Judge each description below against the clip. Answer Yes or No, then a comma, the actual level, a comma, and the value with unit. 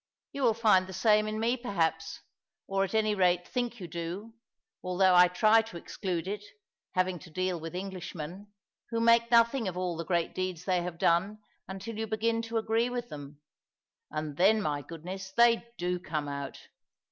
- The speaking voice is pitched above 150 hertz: Yes, high, 190 Hz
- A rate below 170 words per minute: No, average, 180 wpm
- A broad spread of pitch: No, average, 4.3 semitones